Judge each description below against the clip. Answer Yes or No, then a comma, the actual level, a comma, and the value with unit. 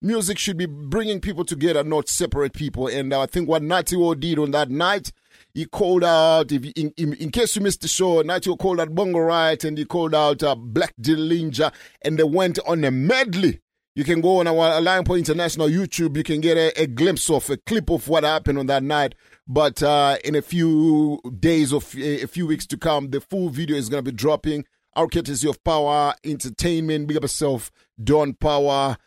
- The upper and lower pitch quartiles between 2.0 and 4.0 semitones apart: Yes, average, 2.7 semitones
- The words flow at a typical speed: No, fast, 215 wpm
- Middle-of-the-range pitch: Yes, medium, 155 Hz